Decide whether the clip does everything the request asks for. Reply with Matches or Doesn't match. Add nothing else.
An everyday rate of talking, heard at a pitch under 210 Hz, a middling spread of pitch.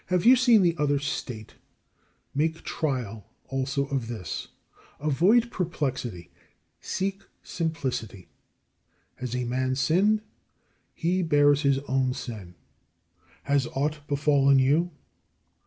Doesn't match